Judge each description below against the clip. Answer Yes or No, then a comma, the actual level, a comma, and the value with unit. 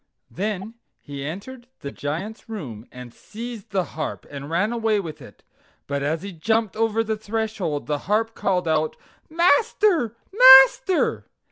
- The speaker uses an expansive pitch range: Yes, wide, 6.4 semitones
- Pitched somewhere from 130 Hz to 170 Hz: No, high, 210 Hz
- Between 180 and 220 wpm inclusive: No, average, 145 wpm